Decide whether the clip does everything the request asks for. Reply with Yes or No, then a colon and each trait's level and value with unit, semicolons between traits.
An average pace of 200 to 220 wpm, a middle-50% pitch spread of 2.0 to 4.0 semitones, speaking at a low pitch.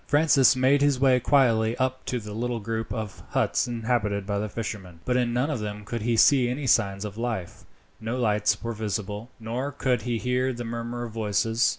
Yes: fast, 205 wpm; average, 2.9 semitones; low, 115 Hz